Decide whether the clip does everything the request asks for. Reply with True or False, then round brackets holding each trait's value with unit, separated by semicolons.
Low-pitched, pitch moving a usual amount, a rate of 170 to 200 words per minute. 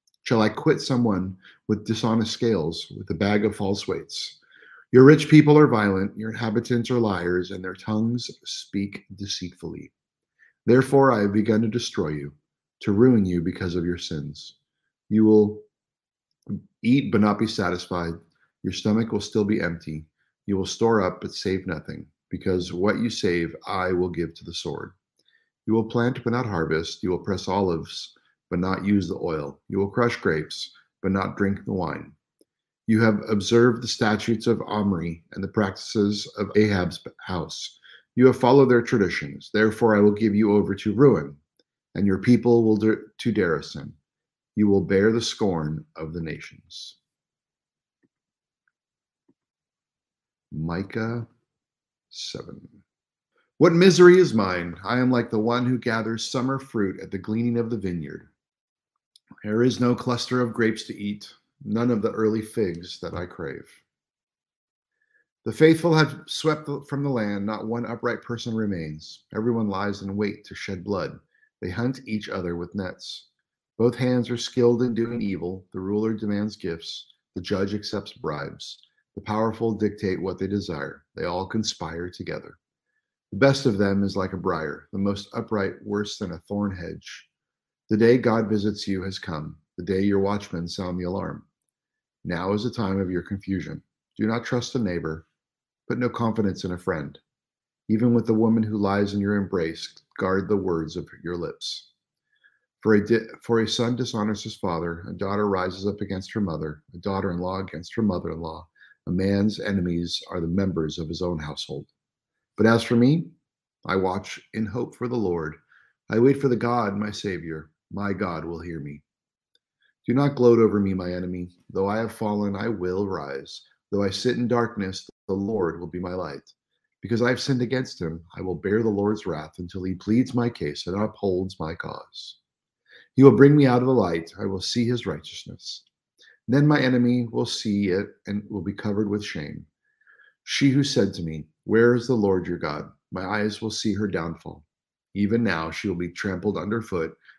True (105 Hz; 3.9 semitones; 175 wpm)